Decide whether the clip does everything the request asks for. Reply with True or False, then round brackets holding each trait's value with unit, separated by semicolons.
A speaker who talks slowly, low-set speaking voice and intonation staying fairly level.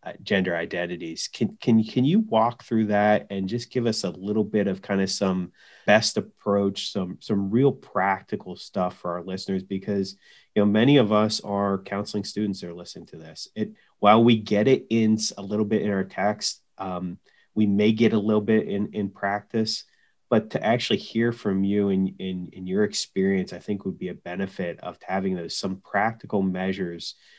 False (200 wpm; 100 Hz; 2.2 semitones)